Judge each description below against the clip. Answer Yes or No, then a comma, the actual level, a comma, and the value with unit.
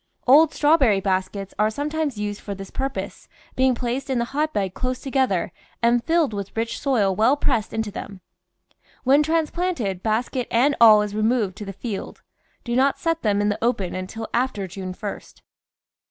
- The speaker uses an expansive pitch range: No, average, 4.9 semitones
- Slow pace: No, average, 170 wpm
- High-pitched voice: Yes, high, 230 Hz